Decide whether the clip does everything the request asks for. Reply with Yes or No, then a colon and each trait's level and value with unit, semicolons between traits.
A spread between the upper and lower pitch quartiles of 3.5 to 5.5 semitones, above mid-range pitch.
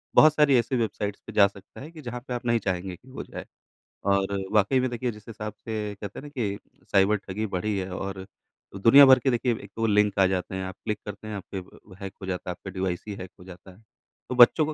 No: average, 3.9 semitones; low, 105 Hz